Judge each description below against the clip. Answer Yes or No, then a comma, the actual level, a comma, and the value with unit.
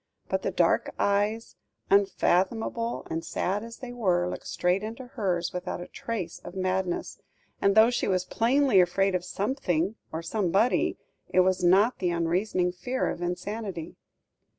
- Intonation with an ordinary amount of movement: Yes, average, 3.9 semitones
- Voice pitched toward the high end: Yes, high, 195 Hz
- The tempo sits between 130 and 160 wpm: Yes, average, 150 wpm